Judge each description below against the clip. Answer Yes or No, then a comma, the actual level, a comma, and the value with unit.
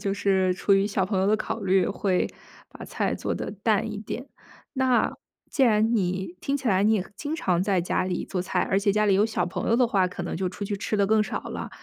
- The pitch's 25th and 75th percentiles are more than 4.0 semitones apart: No, narrow, 2.6 semitones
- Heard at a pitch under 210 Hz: Yes, high, 200 Hz